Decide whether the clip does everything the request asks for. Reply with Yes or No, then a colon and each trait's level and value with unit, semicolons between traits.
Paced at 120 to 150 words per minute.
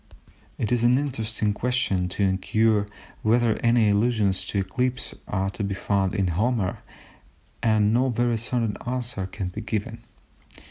Yes: average, 145 wpm